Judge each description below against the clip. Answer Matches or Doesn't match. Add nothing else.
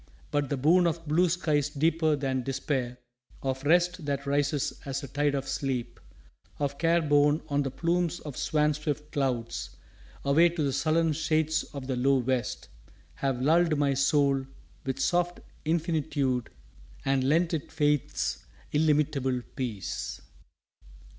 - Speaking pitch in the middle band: Matches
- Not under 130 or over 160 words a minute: Matches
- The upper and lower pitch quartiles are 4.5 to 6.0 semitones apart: Doesn't match